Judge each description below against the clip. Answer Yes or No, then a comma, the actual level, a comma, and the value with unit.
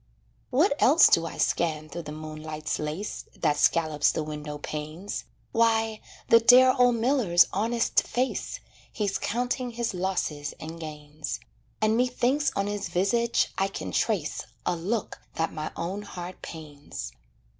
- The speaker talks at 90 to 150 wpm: Yes, average, 145 wpm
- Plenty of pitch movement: Yes, wide, 7.0 semitones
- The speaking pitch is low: No, medium, 185 Hz